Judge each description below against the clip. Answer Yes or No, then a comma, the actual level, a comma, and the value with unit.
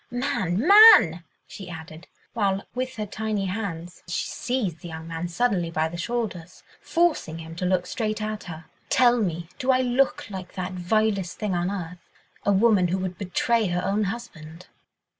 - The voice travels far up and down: No, average, 4.6 semitones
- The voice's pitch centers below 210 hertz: Yes, high, 190 Hz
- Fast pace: No, average, 170 wpm